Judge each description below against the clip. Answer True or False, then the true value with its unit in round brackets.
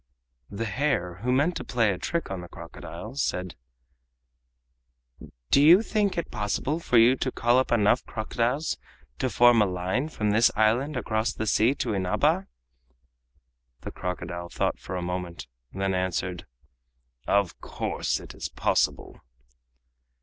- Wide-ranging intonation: True (5.9 semitones)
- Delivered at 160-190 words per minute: False (150 wpm)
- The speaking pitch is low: True (110 Hz)